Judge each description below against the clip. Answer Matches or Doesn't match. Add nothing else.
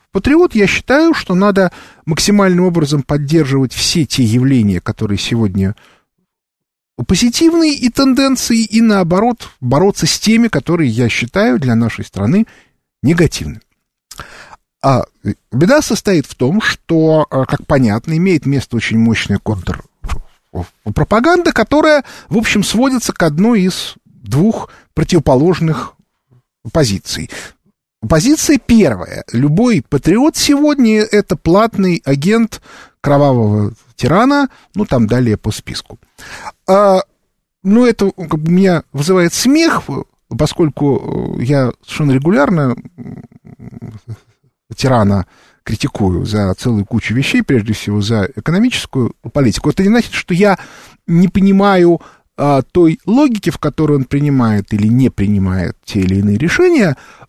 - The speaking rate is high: Doesn't match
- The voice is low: Doesn't match